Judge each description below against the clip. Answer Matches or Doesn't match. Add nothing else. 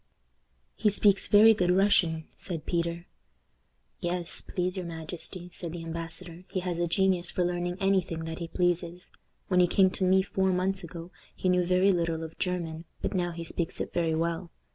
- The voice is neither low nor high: Matches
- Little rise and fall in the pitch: Matches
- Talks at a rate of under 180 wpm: Doesn't match